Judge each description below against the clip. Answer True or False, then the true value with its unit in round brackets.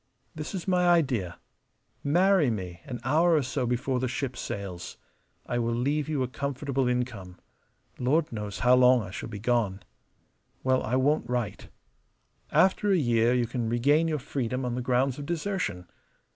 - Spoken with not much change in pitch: False (3.9 semitones)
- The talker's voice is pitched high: False (125 Hz)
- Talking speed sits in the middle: True (170 wpm)